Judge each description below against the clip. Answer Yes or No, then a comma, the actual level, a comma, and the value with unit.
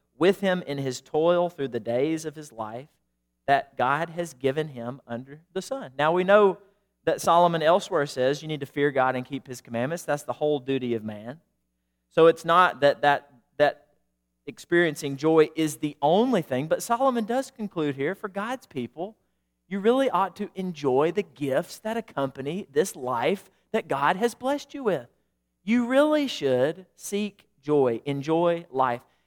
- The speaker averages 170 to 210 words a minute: Yes, average, 175 wpm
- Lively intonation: Yes, wide, 6.6 semitones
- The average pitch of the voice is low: No, medium, 155 Hz